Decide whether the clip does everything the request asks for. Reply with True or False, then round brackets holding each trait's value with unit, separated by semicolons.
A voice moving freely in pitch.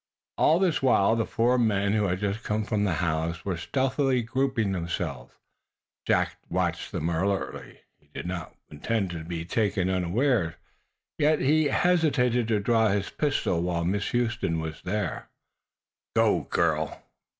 True (6.0 semitones)